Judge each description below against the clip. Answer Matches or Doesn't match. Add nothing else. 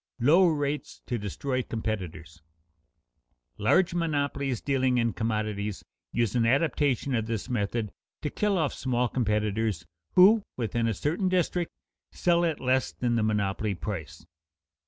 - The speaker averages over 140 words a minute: Doesn't match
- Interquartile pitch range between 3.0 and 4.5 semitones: Doesn't match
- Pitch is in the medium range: Doesn't match